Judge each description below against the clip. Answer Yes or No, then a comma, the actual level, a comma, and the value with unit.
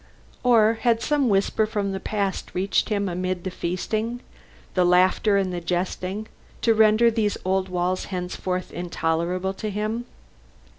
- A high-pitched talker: Yes, high, 195 Hz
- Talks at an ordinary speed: Yes, average, 145 wpm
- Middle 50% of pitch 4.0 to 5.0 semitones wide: No, average, 3.0 semitones